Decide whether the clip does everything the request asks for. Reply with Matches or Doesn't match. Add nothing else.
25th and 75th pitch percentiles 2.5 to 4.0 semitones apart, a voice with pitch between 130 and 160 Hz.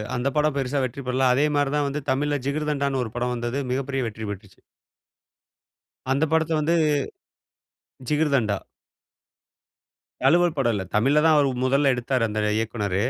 Matches